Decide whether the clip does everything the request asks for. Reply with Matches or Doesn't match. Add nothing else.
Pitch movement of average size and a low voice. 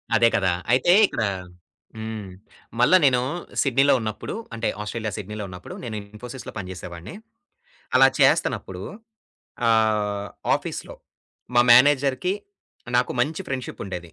Matches